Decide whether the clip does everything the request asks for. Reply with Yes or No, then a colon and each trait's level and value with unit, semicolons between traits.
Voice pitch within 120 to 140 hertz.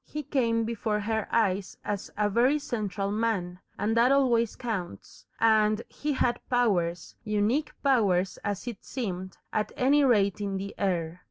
No: high, 215 Hz